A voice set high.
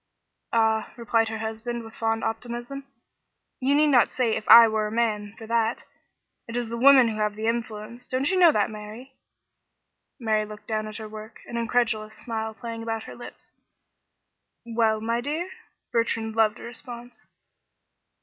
Yes: high, 225 Hz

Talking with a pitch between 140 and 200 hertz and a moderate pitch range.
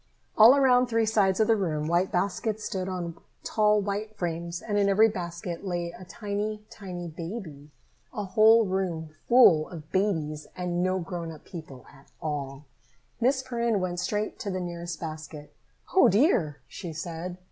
Yes: medium, 185 Hz; average, 4.1 semitones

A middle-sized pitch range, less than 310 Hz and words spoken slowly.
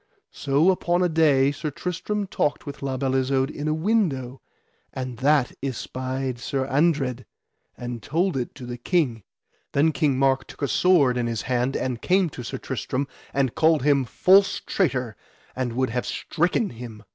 No: average, 3.9 semitones; low, 135 Hz; average, 170 wpm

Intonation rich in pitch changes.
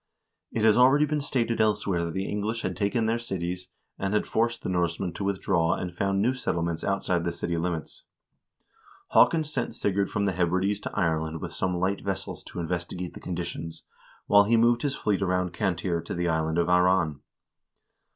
No: average, 3.4 semitones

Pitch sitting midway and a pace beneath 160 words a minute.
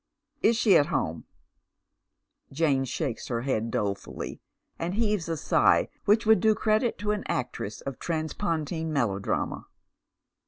Yes: medium, 160 Hz; average, 145 wpm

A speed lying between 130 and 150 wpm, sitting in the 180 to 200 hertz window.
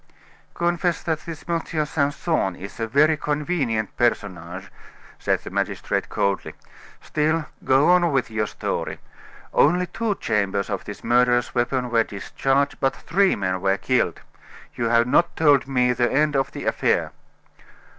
No: average, 145 wpm; low, 135 Hz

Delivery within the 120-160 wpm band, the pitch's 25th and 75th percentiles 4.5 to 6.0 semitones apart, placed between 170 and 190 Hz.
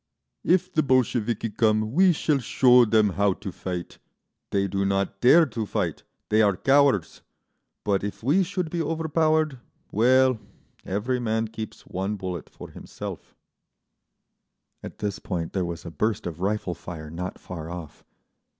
No: average, 150 wpm; wide, 5.4 semitones; low, 110 Hz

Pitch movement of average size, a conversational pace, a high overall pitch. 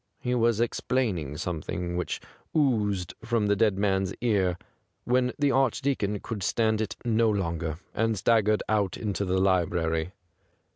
No: average, 4.0 semitones; average, 145 wpm; low, 105 Hz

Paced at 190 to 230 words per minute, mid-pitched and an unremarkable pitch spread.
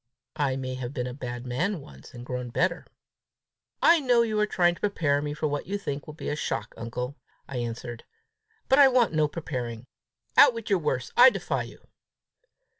No: average, 195 wpm; medium, 145 Hz; wide, 8.1 semitones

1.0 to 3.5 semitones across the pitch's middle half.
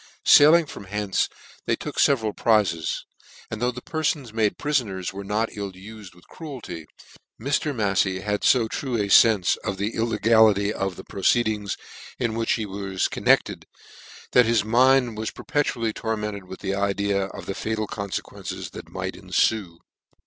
Yes: average, 2.9 semitones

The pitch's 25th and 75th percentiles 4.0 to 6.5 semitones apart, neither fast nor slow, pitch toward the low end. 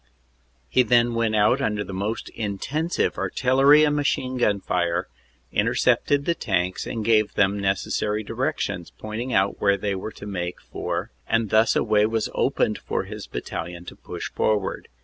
No: average, 3.4 semitones; average, 170 wpm; low, 110 Hz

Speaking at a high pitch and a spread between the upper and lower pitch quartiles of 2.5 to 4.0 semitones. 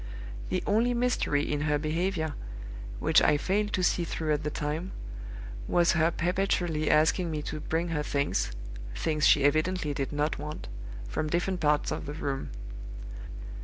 No: medium, 155 Hz; average, 3.1 semitones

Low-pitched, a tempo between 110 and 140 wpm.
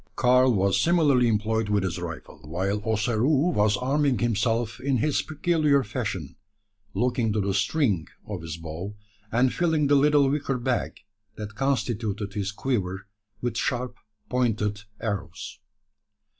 Yes: low, 115 Hz; slow, 135 wpm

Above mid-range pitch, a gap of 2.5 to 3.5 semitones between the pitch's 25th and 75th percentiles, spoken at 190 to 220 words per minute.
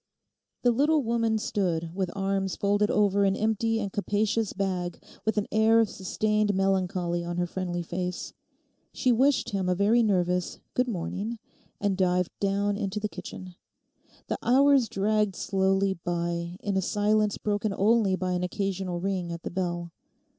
No: high, 195 Hz; average, 2.9 semitones; average, 160 wpm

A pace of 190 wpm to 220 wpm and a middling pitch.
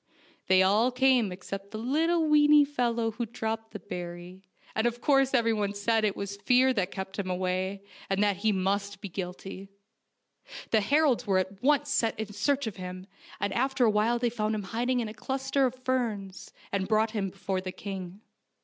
No: average, 195 wpm; high, 215 Hz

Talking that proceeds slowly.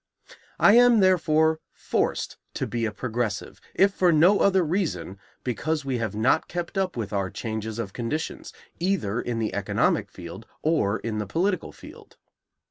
No: average, 160 wpm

